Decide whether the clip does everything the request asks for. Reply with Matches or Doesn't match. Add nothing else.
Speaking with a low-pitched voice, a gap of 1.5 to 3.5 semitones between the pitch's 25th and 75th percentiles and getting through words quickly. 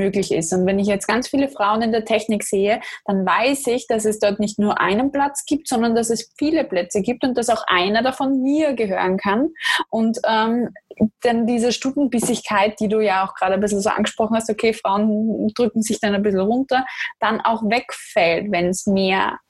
Doesn't match